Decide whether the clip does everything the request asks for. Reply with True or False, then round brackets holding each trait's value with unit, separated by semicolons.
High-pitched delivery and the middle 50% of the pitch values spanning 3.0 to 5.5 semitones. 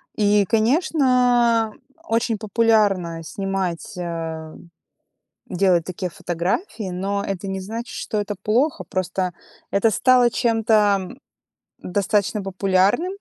True (200 Hz; 3.6 semitones)